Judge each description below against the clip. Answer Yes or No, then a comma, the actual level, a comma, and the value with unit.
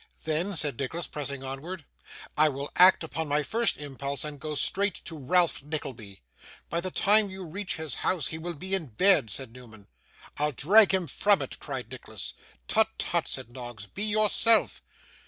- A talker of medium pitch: Yes, medium, 155 Hz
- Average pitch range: No, wide, 5.7 semitones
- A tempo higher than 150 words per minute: Yes, average, 175 wpm